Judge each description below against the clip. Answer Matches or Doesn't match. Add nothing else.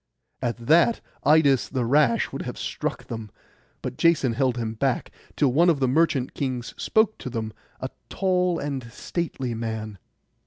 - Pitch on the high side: Doesn't match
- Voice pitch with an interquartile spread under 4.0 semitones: Doesn't match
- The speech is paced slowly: Doesn't match